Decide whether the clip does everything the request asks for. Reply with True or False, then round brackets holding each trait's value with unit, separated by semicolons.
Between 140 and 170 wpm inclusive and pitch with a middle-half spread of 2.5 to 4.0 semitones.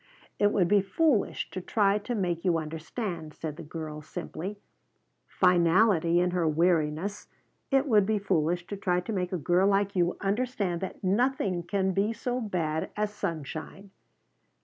True (160 wpm; 3.5 semitones)